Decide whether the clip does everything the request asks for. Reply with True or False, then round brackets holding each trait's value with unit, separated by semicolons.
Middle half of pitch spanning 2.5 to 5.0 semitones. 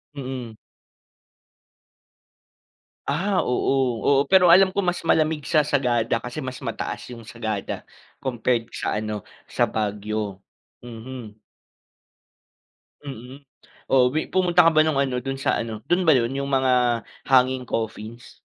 True (4.2 semitones)